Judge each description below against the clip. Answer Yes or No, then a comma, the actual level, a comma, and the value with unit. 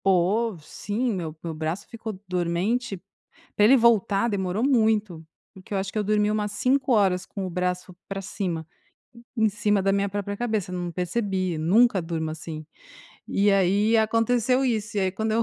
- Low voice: No, high, 200 Hz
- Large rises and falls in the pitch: No, average, 3.3 semitones